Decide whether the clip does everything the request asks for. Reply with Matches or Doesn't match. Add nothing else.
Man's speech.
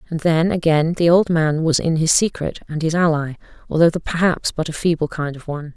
Doesn't match